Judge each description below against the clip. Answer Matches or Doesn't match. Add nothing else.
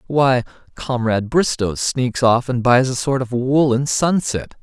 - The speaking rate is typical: Matches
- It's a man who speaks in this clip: Matches